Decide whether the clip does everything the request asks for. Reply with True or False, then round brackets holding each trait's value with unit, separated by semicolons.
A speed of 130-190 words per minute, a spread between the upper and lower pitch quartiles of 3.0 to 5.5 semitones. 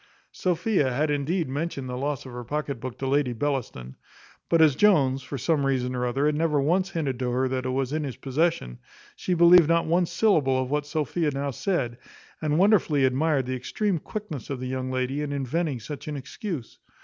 False (205 wpm; 3.9 semitones)